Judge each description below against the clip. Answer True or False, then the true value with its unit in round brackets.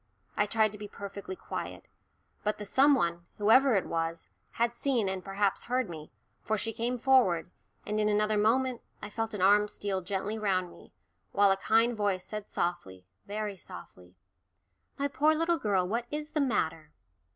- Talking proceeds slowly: False (175 wpm)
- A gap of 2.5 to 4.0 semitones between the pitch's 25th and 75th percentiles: True (3.6 semitones)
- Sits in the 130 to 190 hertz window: False (210 Hz)